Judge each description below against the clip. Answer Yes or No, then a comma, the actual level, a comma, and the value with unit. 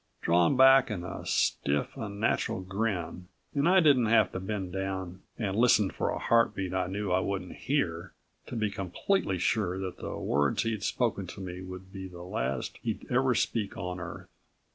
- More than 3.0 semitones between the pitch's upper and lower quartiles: Yes, average, 3.8 semitones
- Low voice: Yes, very low, 95 Hz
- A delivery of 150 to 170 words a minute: No, average, 180 wpm